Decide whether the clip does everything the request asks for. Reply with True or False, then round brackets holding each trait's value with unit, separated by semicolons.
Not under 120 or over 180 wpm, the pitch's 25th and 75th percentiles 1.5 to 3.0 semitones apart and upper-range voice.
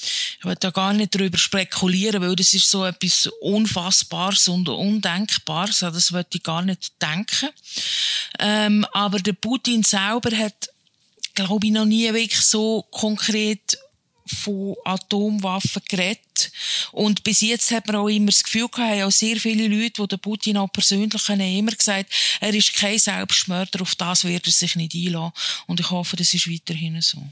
True (175 wpm; 2.7 semitones; 200 Hz)